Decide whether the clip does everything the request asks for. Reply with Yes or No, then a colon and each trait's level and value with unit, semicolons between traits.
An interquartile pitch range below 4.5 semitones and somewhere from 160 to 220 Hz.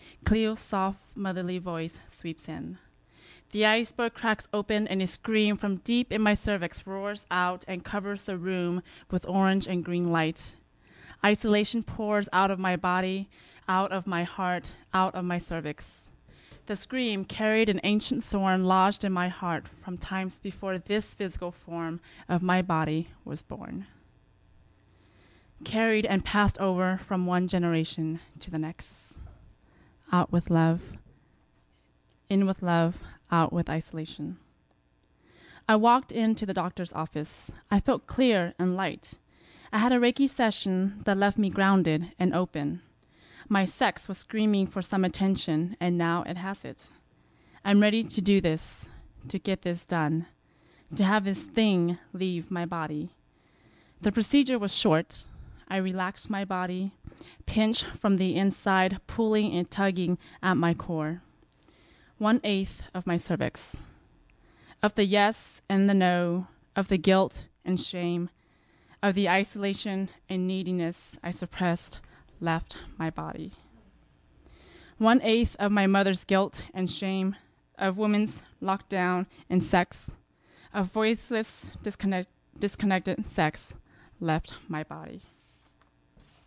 Yes: average, 3.0 semitones; medium, 185 Hz